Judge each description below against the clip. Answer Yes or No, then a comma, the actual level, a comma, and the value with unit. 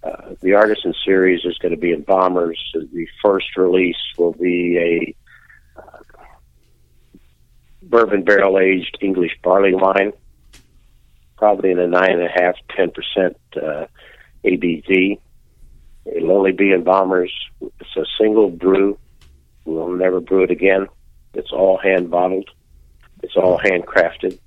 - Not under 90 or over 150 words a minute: Yes, slow, 135 wpm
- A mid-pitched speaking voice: No, very low, 90 Hz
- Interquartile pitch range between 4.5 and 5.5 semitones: Yes, average, 4.9 semitones